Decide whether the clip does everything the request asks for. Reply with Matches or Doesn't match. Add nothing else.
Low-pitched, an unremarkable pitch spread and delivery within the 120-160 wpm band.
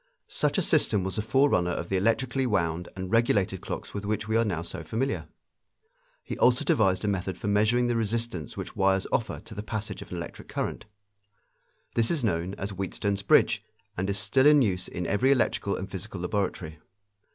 Doesn't match